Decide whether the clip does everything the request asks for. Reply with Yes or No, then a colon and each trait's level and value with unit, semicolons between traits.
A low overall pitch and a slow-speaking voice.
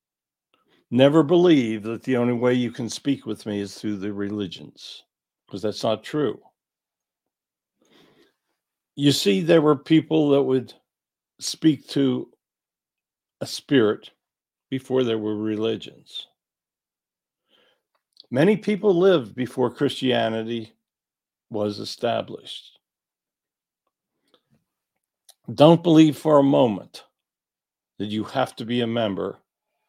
Yes: low, 125 Hz; slow, 105 wpm